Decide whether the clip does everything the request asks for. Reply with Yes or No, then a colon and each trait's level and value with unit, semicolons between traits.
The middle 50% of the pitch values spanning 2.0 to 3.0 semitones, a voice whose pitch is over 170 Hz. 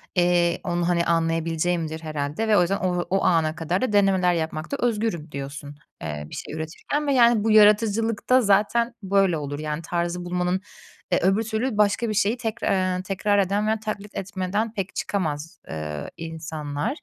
No: average, 4.4 semitones; medium, 185 Hz